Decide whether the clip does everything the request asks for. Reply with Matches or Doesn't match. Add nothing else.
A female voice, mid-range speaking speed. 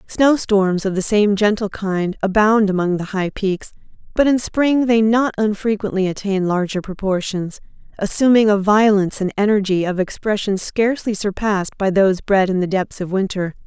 Matches